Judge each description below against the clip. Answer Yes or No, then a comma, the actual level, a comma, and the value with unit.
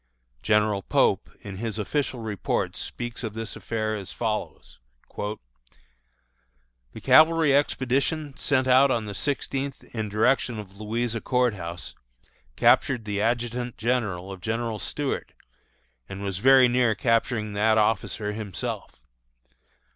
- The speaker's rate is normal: No, slow, 125 wpm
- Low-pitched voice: Yes, low, 110 Hz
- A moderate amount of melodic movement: Yes, average, 3.8 semitones